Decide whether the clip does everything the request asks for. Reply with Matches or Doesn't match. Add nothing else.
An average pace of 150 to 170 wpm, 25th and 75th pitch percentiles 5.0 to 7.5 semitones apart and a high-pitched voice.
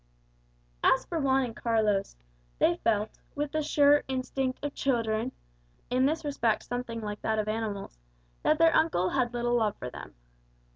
Doesn't match